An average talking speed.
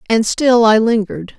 Yes: average, 175 wpm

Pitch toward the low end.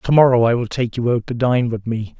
Yes: low, 120 Hz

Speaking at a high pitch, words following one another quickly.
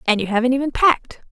Yes: very high, 250 Hz; fast, 230 wpm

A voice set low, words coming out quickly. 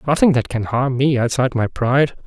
Yes: low, 130 Hz; fast, 210 wpm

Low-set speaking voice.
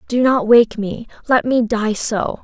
No: high, 230 Hz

